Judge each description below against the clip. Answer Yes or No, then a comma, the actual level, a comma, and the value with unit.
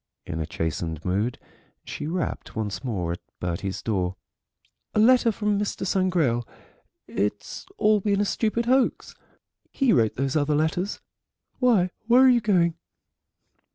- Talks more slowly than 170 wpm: Yes, average, 140 wpm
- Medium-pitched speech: Yes, medium, 170 Hz